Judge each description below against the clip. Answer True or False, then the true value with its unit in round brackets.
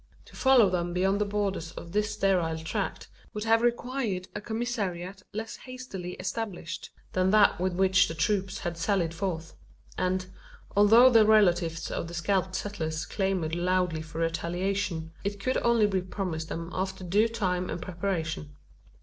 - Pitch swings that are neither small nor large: True (3.4 semitones)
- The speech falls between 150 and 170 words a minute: True (160 wpm)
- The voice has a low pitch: False (185 Hz)